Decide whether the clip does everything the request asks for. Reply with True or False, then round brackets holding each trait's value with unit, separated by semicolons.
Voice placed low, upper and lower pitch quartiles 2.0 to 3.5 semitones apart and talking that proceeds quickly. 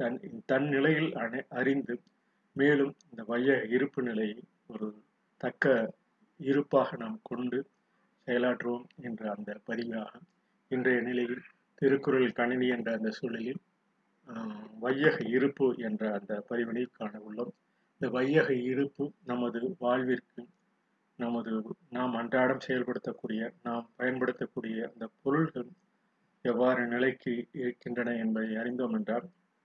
False (125 Hz; 2.7 semitones; 105 wpm)